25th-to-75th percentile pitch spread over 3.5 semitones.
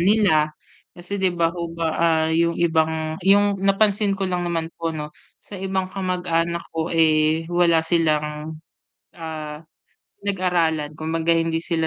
No: narrow, 2.4 semitones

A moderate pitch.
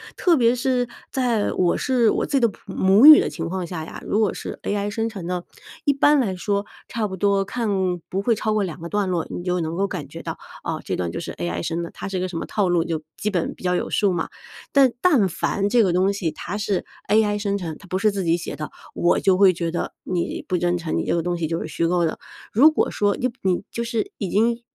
No: high, 195 Hz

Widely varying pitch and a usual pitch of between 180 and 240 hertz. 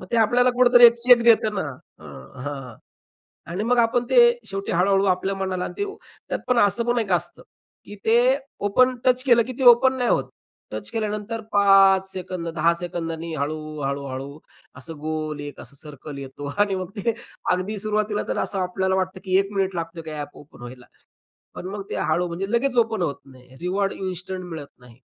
Yes: wide, 5.8 semitones; high, 190 Hz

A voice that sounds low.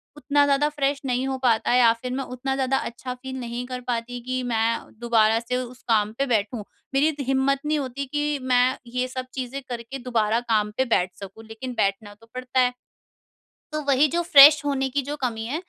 No: very high, 255 Hz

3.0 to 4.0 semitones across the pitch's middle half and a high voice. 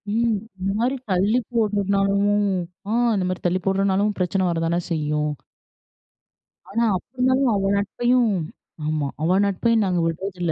Yes: average, 3.4 semitones; high, 195 Hz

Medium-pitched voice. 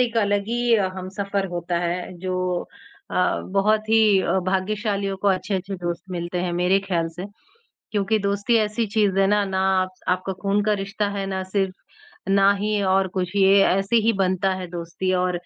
No: high, 195 Hz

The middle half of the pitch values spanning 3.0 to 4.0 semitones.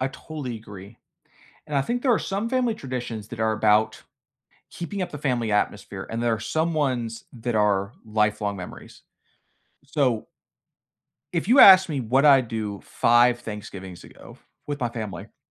No: wide, 5.4 semitones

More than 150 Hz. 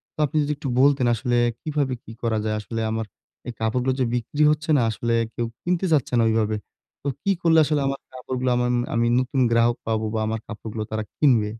No: low, 125 Hz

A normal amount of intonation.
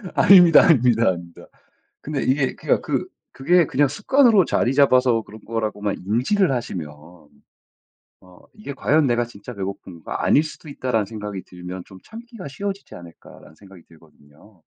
No: wide, 7.8 semitones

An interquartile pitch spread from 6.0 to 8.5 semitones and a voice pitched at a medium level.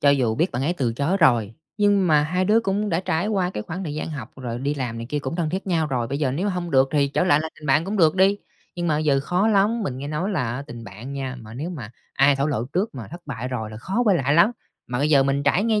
No: wide, 5.5 semitones; medium, 150 Hz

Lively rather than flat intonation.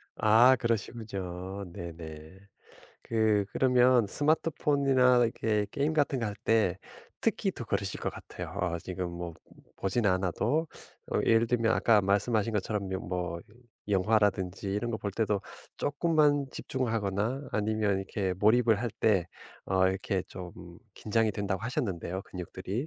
No: average, 4.0 semitones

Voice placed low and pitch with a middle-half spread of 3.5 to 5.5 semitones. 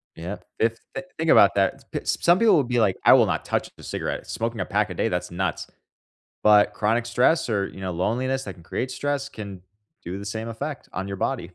Yes: low, 105 Hz; average, 4.9 semitones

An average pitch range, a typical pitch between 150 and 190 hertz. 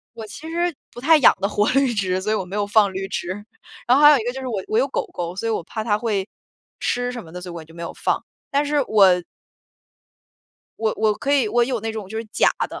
No: average, 4.6 semitones; high, 220 Hz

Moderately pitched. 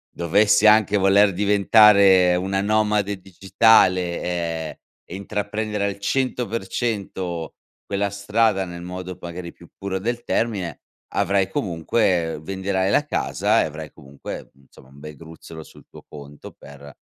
No: very low, 95 Hz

